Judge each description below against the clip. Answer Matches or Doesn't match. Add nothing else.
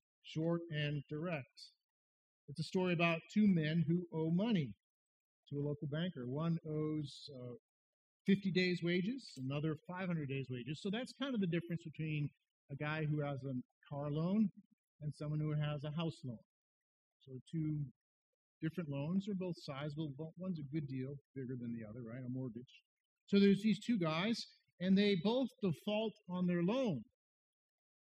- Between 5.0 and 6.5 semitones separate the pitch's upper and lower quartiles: Doesn't match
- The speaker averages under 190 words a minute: Matches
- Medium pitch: Matches